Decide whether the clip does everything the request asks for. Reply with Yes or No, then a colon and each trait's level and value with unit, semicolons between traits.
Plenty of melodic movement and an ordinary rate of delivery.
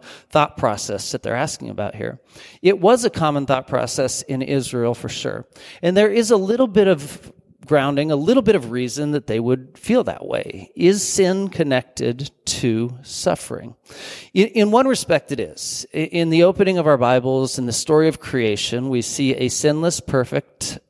Yes: wide, 6.9 semitones; average, 180 wpm